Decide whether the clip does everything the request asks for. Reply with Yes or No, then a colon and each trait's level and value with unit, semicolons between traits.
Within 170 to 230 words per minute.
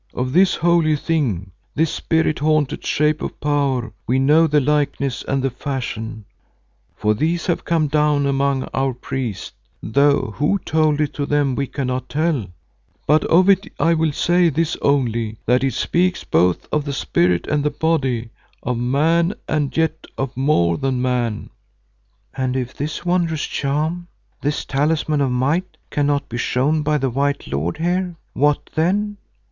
No: average, 160 wpm